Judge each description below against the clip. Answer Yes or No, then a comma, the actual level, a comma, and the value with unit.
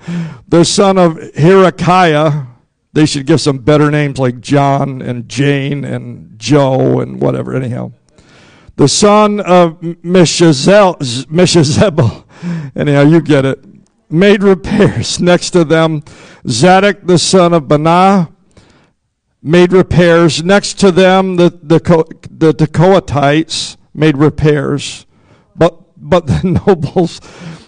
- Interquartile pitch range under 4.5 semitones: Yes, average, 4.1 semitones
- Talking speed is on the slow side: Yes, slow, 115 wpm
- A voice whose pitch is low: No, medium, 165 Hz